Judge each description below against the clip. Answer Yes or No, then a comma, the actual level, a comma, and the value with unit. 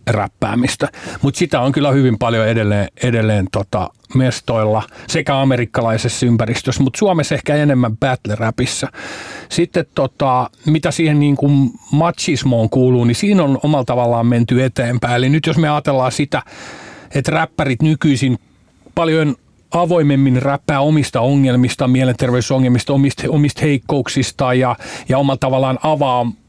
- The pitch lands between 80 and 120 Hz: No, low, 135 Hz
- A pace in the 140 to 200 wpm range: No, average, 130 wpm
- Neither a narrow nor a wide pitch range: Yes, average, 3.4 semitones